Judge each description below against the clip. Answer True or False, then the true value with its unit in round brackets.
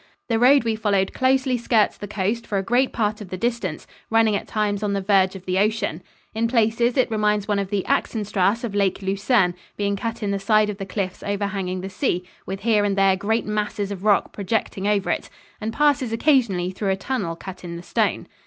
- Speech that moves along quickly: True (220 wpm)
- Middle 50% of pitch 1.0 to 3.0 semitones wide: True (2.7 semitones)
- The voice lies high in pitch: True (205 Hz)